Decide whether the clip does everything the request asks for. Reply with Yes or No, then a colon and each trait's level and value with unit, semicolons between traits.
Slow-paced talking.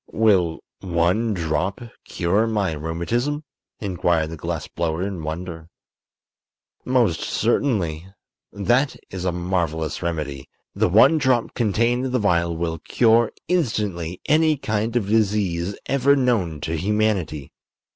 Yes: slow, 125 wpm